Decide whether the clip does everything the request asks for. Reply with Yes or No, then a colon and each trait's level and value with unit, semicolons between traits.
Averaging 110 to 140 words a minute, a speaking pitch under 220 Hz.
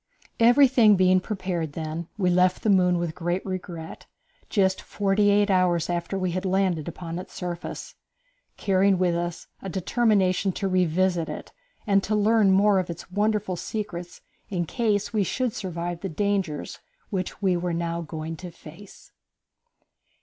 No: average, 155 wpm; medium, 185 Hz